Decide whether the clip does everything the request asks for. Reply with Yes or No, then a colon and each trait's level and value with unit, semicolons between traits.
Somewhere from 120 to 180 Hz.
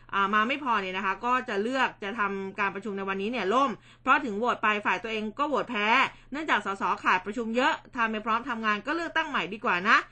No: high, 220 Hz